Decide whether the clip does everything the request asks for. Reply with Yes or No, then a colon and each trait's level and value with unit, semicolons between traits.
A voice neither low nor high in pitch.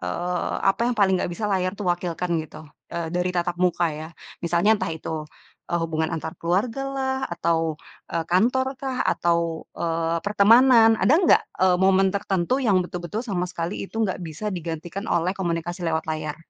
Yes: medium, 180 Hz